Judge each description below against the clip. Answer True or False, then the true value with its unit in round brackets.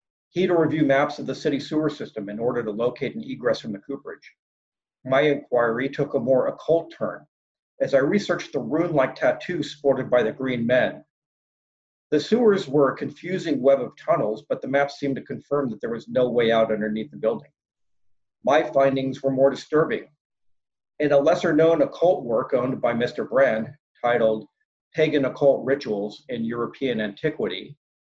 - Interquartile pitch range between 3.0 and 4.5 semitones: True (4.2 semitones)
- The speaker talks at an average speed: True (175 wpm)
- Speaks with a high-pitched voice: False (135 Hz)